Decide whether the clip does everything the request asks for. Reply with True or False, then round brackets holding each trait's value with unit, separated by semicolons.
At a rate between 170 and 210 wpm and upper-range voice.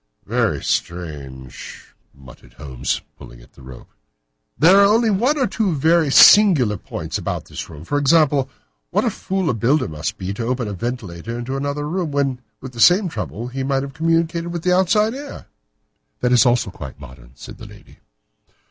False (180 wpm; 135 Hz)